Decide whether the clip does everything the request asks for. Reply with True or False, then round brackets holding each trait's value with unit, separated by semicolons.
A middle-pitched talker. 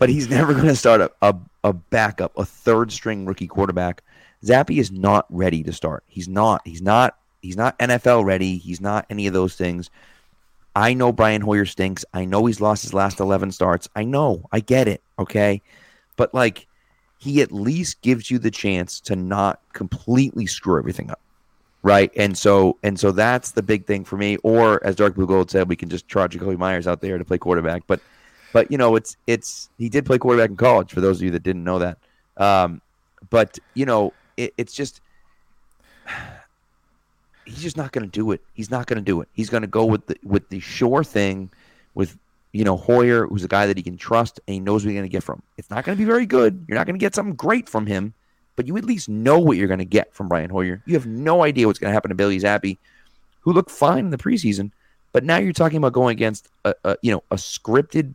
False (105 Hz)